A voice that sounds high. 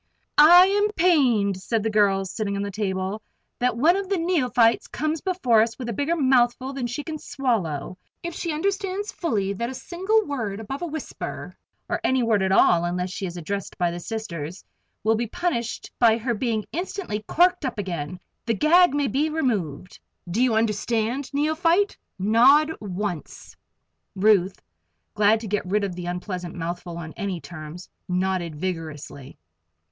Yes: high, 225 Hz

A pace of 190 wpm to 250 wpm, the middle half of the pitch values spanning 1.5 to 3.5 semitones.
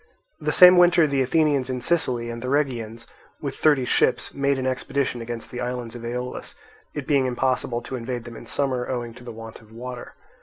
Yes: average, 200 wpm; average, 2.7 semitones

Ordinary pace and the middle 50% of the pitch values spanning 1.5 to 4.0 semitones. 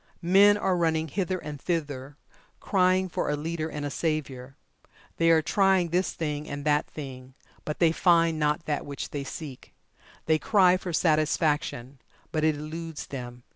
Yes: average, 165 wpm; average, 2.8 semitones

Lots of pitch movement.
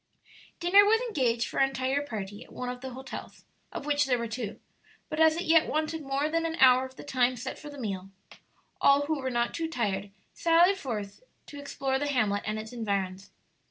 No: average, 4.8 semitones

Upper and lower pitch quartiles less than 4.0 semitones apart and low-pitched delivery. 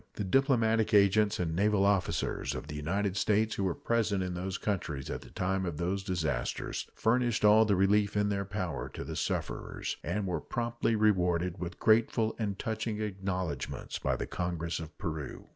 Yes: average, 3.2 semitones; low, 100 Hz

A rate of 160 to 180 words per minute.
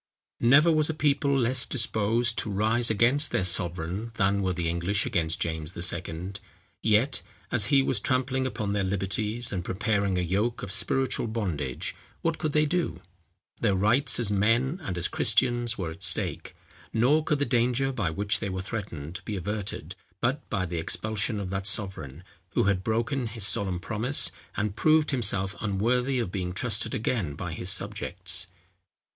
Yes: average, 170 wpm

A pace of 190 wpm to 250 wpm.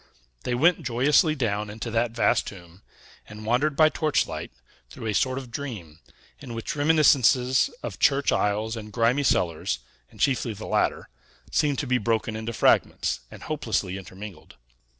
No: average, 155 wpm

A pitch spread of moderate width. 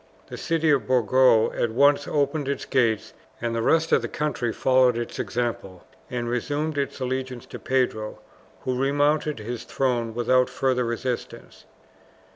Yes: average, 3.0 semitones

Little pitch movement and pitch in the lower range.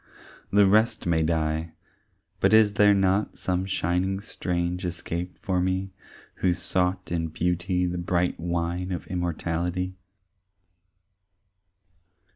Yes: narrow, 1.5 semitones; very low, 90 Hz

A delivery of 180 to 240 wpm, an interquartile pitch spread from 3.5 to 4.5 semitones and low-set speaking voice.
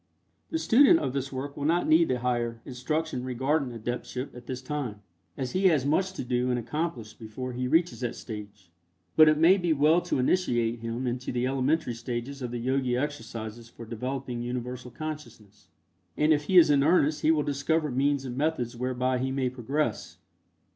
Yes: average, 190 wpm; average, 3.8 semitones; low, 130 Hz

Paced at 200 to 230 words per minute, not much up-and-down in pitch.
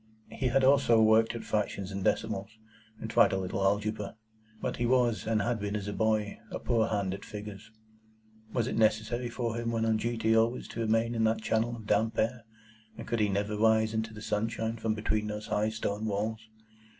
Yes: fast, 205 wpm; narrow, 1.5 semitones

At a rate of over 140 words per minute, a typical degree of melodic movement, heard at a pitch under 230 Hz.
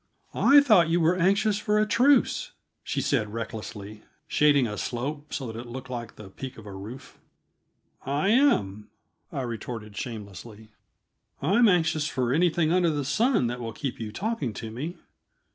No: average, 165 wpm; wide, 7.6 semitones; low, 135 Hz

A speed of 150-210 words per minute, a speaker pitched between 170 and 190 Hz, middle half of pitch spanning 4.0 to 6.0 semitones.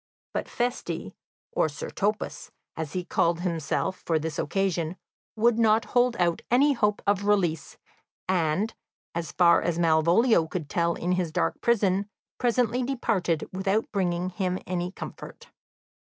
No: average, 140 wpm; medium, 185 Hz; average, 4.5 semitones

